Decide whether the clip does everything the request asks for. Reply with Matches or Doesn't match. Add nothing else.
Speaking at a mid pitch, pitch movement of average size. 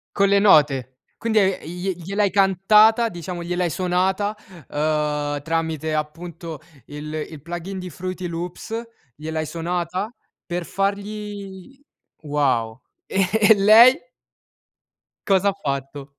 Matches